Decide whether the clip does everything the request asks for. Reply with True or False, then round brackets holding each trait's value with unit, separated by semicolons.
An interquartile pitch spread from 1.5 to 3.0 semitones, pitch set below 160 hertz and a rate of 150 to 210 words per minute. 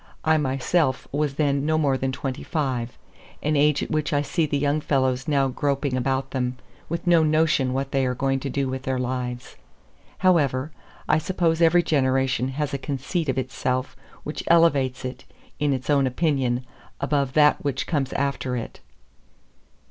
True (2.6 semitones; 140 Hz; 170 wpm)